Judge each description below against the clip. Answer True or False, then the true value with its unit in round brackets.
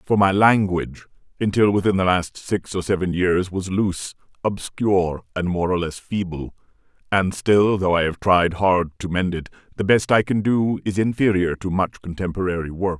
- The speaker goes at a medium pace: True (185 wpm)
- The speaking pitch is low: True (95 Hz)